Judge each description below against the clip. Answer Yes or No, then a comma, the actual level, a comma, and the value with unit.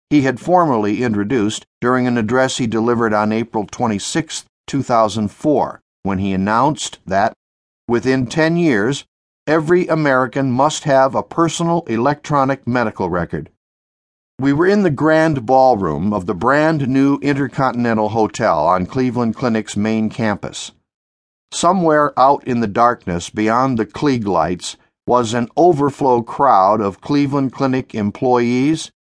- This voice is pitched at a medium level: No, low, 125 Hz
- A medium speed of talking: No, slow, 130 wpm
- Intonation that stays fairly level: No, average, 4.9 semitones